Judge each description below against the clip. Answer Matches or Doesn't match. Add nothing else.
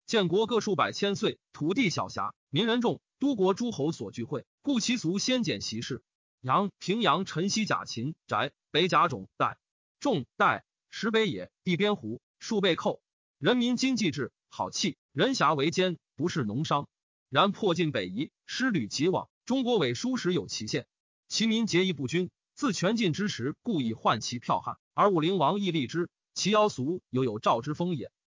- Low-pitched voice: Doesn't match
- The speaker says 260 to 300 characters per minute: Doesn't match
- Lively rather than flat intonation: Matches